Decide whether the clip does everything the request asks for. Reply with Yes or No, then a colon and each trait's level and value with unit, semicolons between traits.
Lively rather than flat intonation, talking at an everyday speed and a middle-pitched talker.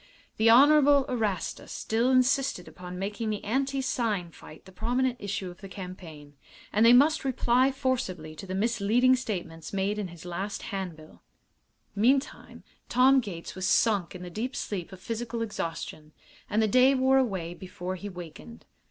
No: wide, 5.8 semitones; average, 165 wpm; high, 210 Hz